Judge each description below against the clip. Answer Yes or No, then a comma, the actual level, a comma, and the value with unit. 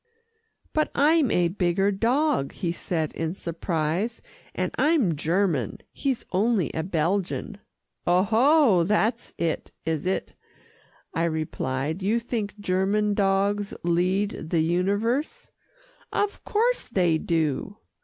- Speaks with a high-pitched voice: Yes, high, 195 Hz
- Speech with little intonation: No, average, 5.1 semitones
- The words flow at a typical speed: No, slow, 115 wpm